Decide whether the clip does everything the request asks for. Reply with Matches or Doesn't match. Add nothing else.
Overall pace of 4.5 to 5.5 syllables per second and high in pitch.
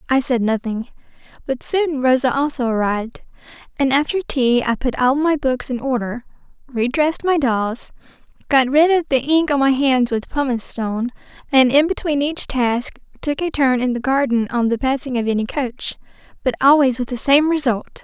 Matches